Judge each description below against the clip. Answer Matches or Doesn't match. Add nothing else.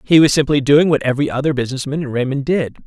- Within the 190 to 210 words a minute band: Doesn't match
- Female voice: Doesn't match